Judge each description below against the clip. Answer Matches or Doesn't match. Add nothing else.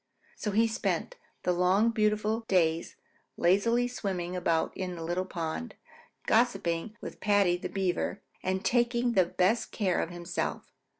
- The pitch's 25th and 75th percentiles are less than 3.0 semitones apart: Doesn't match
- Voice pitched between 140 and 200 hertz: Matches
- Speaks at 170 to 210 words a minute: Doesn't match